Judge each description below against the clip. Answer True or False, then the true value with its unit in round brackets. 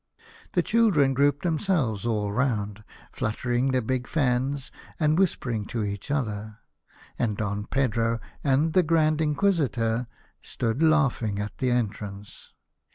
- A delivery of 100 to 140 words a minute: True (135 wpm)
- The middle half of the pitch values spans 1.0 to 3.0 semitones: False (5.5 semitones)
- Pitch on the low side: True (125 Hz)